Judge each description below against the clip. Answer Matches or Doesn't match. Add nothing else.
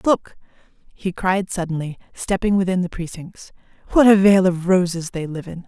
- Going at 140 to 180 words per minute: Matches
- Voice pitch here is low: Doesn't match